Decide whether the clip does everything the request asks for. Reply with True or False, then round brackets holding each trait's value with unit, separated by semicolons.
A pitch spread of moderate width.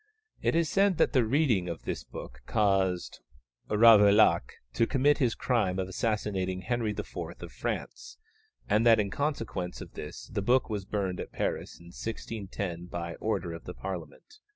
True (4.4 semitones)